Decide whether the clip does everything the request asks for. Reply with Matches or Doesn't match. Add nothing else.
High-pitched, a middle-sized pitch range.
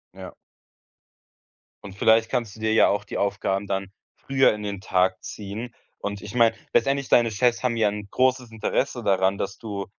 Doesn't match